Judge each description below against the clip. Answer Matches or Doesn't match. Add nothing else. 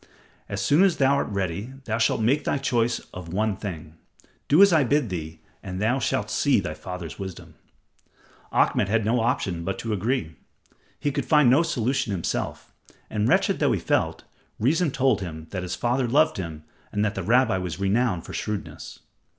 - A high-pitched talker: Doesn't match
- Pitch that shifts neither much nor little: Doesn't match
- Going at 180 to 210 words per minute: Matches